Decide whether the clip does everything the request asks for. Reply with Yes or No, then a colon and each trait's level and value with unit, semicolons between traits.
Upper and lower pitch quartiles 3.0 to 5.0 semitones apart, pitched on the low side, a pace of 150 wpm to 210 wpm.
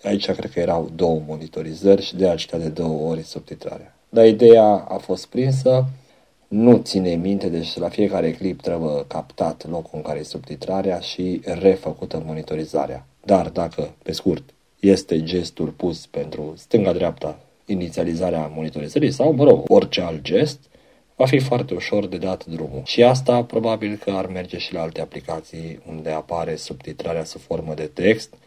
No: wide, 5.5 semitones; very low, 90 Hz; average, 160 wpm